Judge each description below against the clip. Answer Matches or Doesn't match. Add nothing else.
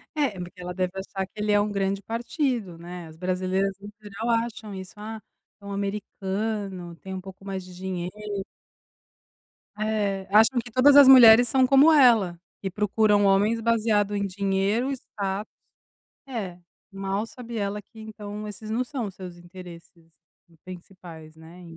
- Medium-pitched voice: Doesn't match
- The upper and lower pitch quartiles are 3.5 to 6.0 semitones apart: Doesn't match